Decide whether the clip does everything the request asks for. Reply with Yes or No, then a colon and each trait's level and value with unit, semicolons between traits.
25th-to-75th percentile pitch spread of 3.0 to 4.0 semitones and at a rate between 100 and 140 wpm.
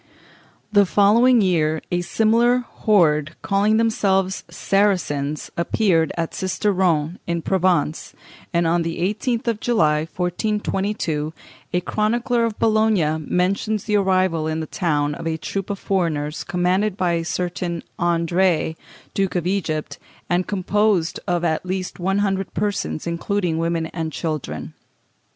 Yes: average, 3.7 semitones; slow, 135 wpm